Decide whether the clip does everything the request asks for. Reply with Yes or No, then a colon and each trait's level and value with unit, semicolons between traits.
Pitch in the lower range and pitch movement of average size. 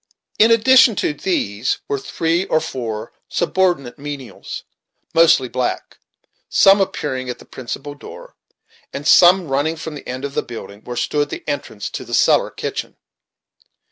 No: medium, 145 Hz; average, 5.0 semitones